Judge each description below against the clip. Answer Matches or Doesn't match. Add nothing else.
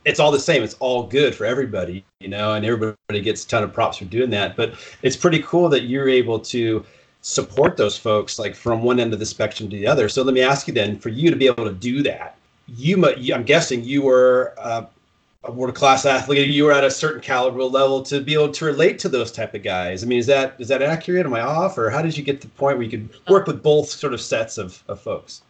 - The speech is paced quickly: Matches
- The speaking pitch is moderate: Doesn't match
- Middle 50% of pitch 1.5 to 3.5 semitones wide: Doesn't match